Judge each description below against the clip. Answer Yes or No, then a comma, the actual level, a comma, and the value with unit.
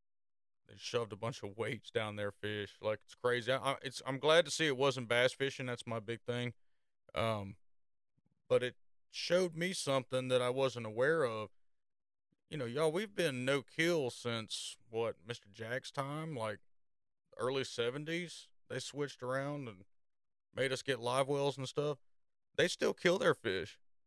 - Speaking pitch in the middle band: No, low, 130 Hz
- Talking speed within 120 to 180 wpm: Yes, average, 170 wpm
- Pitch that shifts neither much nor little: Yes, average, 3.9 semitones